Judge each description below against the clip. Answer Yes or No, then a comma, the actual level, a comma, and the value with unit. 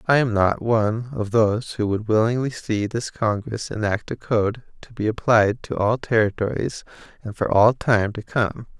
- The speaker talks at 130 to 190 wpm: Yes, average, 185 wpm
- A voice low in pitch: Yes, low, 110 Hz